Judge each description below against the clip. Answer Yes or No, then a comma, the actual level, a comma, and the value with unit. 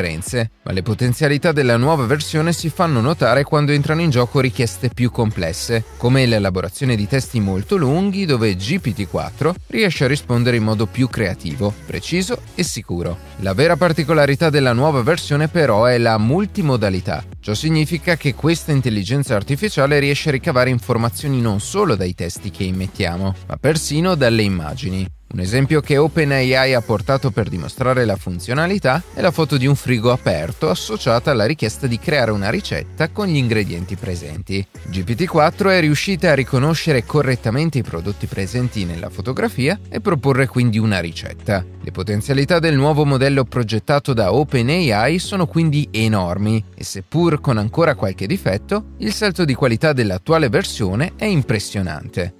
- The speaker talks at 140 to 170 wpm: Yes, average, 150 wpm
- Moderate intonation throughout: No, wide, 6.5 semitones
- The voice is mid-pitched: No, low, 125 Hz